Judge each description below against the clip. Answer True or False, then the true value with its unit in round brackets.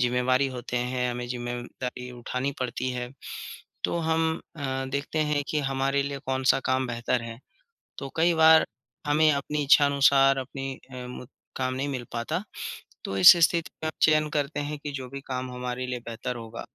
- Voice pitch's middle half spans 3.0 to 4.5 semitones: False (2.6 semitones)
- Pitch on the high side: False (130 Hz)